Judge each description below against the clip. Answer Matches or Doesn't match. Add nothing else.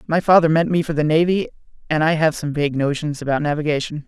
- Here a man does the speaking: Matches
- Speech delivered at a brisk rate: Matches